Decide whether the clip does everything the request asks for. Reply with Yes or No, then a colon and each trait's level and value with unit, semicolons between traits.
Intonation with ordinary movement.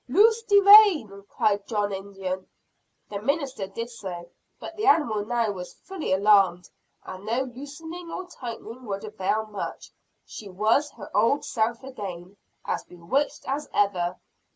No: wide, 6.3 semitones